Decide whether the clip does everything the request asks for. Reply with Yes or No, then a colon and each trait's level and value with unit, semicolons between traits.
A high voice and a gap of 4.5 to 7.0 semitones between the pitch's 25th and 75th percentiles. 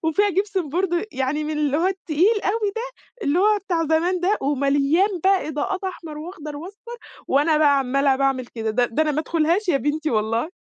Yes: very high, 315 Hz; average, 4.9 semitones